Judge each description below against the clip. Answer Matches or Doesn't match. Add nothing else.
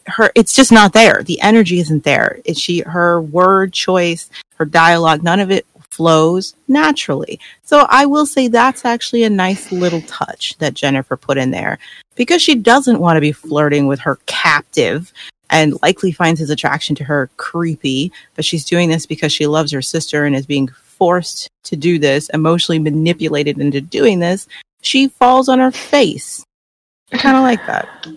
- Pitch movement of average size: Doesn't match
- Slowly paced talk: Doesn't match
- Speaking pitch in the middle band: Matches